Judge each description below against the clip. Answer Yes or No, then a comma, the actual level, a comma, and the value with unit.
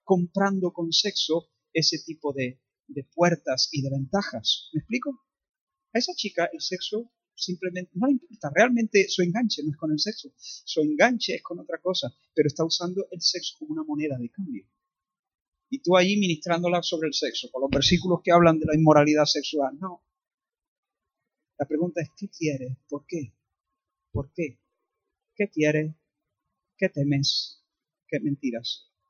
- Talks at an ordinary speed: Yes, average, 160 wpm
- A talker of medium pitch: Yes, medium, 175 Hz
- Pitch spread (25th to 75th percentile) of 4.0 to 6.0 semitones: Yes, wide, 5.4 semitones